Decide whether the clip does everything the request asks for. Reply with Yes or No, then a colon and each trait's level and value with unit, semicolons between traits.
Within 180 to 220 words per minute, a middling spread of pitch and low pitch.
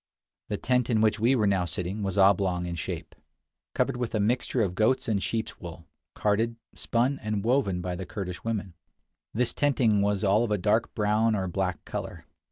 Yes: average, 190 wpm; average, 3.3 semitones; low, 105 Hz